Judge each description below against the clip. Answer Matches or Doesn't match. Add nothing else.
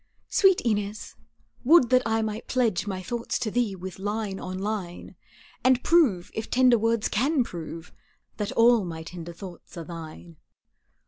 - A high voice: Matches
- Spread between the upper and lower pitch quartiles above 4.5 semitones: Matches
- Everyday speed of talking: Matches